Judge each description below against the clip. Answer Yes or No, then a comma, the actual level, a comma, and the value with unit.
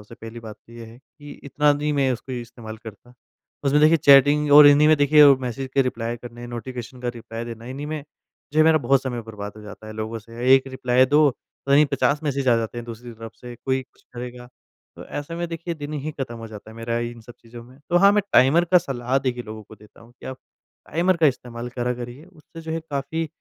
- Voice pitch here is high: No, low, 125 Hz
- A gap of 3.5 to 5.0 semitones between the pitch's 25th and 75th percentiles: Yes, average, 3.8 semitones